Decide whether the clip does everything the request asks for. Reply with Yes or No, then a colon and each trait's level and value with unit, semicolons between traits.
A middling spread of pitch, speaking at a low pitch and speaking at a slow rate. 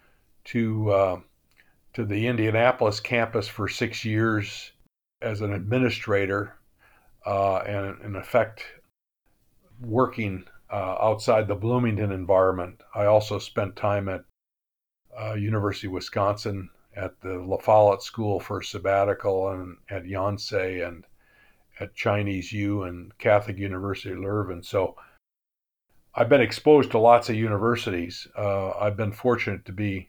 No: narrow, 2.3 semitones; low, 100 Hz; slow, 130 wpm